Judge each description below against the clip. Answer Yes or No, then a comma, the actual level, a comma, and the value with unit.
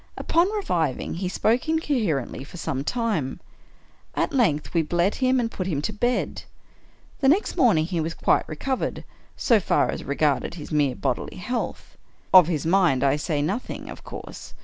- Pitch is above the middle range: No, medium, 180 Hz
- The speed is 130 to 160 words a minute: No, average, 170 wpm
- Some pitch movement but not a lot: No, wide, 8.1 semitones